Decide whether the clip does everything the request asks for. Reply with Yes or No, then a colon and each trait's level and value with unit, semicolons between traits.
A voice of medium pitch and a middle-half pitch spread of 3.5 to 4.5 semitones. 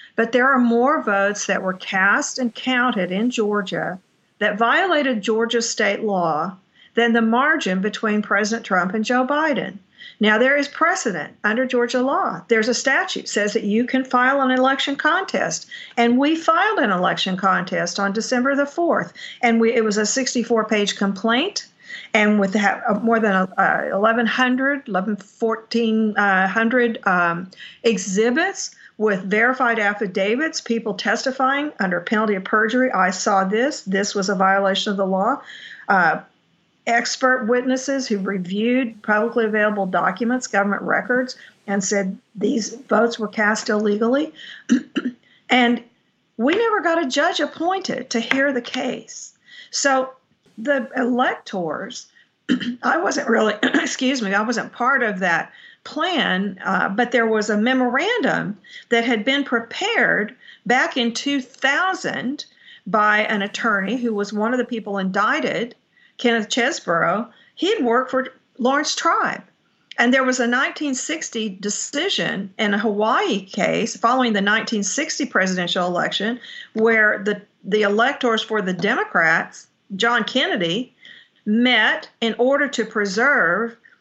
No: high, 230 Hz; average, 3.9 semitones